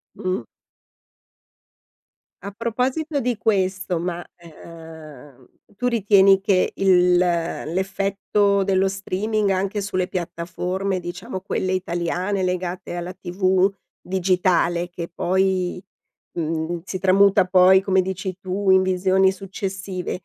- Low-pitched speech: No, medium, 185 Hz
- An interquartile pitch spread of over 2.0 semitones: No, narrow, 1.7 semitones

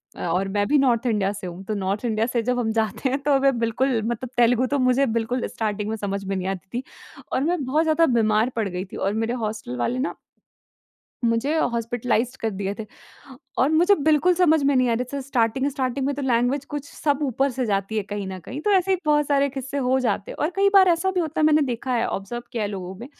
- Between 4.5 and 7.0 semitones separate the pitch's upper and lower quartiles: Yes, average, 4.8 semitones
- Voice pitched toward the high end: Yes, high, 245 Hz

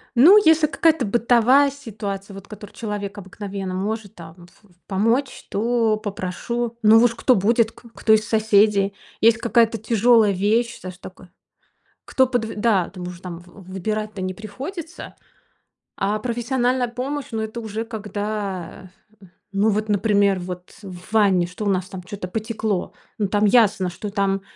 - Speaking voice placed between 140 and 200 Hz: No, high, 210 Hz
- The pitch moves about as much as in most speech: Yes, average, 3.1 semitones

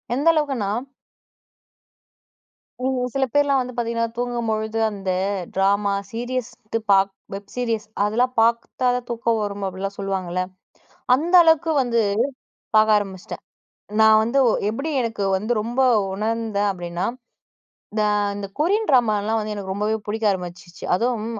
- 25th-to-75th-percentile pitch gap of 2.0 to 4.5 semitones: Yes, average, 3.5 semitones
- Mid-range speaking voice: No, high, 220 Hz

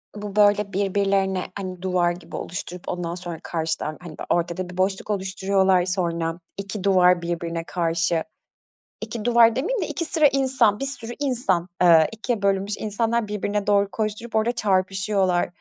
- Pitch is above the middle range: Yes, high, 195 Hz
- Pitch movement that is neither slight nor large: Yes, average, 3.1 semitones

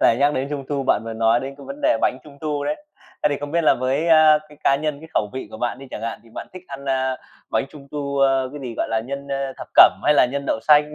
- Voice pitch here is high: No, medium, 140 Hz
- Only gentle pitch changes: Yes, narrow, 2.2 semitones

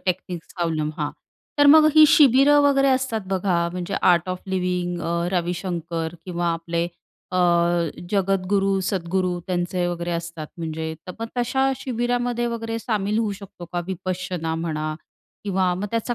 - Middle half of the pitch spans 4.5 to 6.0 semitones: Yes, average, 4.8 semitones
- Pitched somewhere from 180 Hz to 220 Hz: Yes, medium, 185 Hz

